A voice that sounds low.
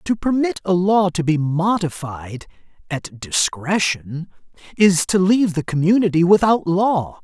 No: medium, 175 Hz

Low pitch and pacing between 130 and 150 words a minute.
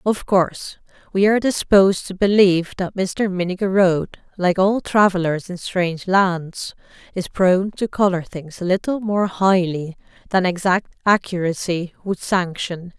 No: medium, 185 Hz; average, 140 wpm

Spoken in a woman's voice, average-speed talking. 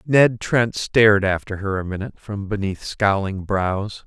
No: male; average, 160 wpm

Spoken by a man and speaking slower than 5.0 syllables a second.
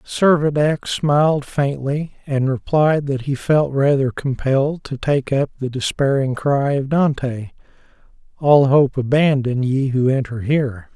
Yes: male; 4.1 syllables/s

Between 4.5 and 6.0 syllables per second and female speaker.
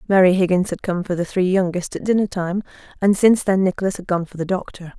No: 6.4 syllables/s; female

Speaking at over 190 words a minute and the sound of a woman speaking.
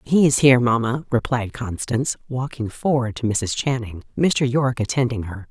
No: average, 165 wpm; female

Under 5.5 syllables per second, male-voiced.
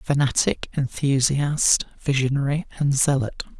Yes: 4.3 syllables/s; male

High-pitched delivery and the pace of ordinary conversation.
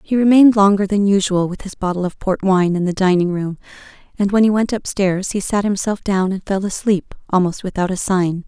No: high, 195 Hz; fast, 220 wpm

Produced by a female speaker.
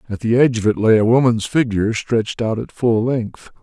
No: male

